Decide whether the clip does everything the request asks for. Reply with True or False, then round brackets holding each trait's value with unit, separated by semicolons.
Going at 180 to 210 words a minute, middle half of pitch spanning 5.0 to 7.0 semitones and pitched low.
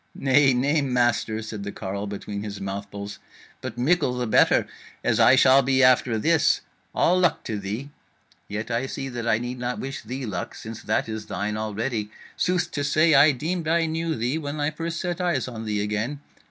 True (195 wpm; 5.4 semitones; 125 Hz)